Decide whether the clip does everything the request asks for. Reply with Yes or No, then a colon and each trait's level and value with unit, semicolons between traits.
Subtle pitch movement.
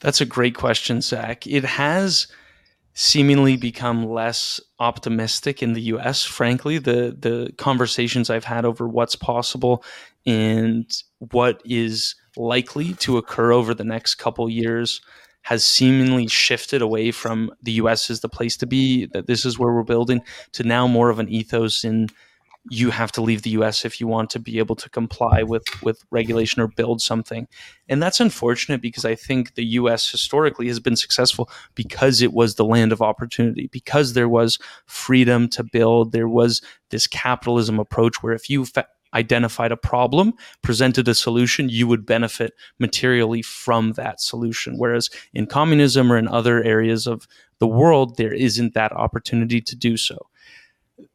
Yes: narrow, 1.6 semitones